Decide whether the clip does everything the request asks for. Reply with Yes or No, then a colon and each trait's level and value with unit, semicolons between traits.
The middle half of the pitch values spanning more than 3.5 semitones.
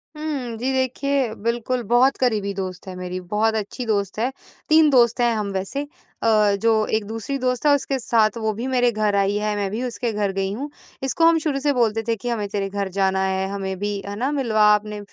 Yes: average, 4.1 semitones